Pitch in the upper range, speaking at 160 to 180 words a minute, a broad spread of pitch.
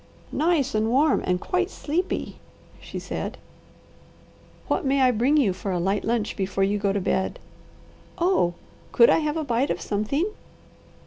Yes: high, 245 Hz; average, 165 wpm; wide, 7.3 semitones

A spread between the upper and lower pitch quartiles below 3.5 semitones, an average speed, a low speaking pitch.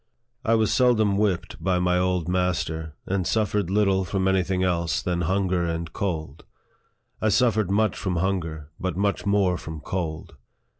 Yes: average, 2.8 semitones; average, 165 wpm; very low, 95 Hz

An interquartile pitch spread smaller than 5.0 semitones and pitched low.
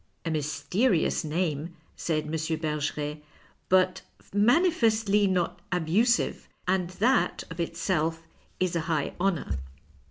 No: average, 4.0 semitones; medium, 170 Hz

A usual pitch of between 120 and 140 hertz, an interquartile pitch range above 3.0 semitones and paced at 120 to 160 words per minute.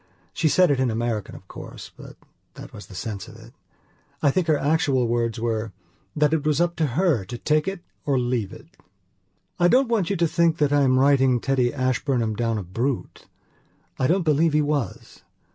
No: low, 135 Hz; average, 5.0 semitones; average, 200 wpm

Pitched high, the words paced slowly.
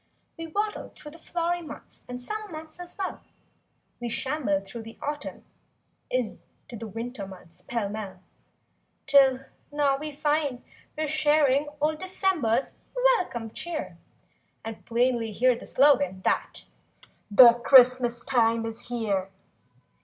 Yes: very high, 255 Hz; slow, 130 wpm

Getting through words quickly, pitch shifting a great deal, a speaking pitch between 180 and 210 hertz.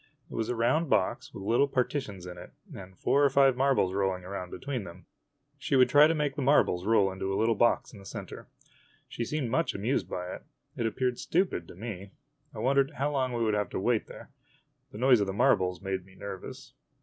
No: fast, 230 wpm; wide, 5.8 semitones; low, 115 Hz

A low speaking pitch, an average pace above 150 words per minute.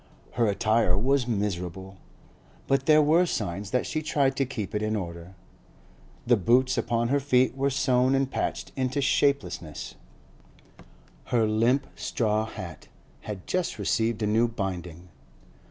No: low, 115 Hz; average, 140 wpm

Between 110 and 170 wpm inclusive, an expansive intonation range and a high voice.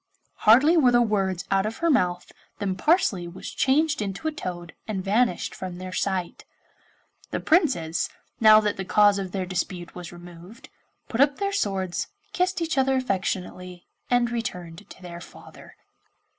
Yes: average, 160 wpm; wide, 5.7 semitones; high, 195 Hz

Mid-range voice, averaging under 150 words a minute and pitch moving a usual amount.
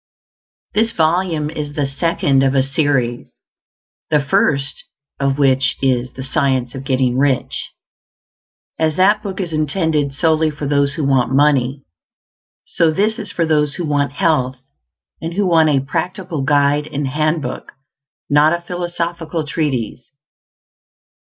Yes: medium, 150 Hz; average, 140 wpm; average, 3.3 semitones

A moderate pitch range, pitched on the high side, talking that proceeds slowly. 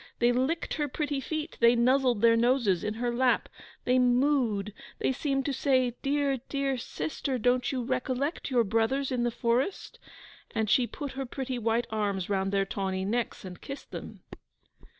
No: average, 3.1 semitones; high, 245 Hz; average, 170 wpm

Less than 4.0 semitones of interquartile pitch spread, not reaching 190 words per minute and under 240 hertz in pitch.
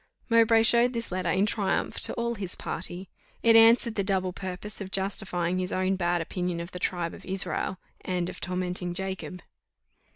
Yes: average, 2.7 semitones; average, 175 wpm; medium, 185 Hz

